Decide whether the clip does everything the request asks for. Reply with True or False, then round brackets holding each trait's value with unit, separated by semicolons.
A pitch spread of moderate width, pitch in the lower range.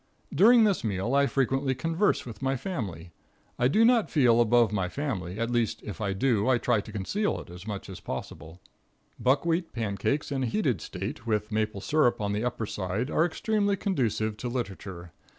False (5.8 semitones; 120 Hz)